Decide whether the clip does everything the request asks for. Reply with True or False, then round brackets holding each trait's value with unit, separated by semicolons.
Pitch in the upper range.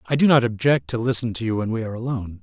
False (115 Hz)